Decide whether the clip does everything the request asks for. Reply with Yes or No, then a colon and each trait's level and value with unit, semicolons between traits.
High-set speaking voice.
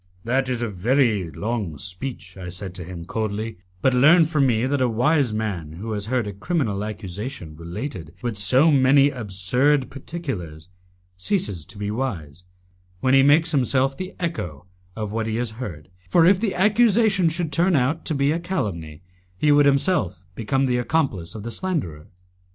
No: low, 120 Hz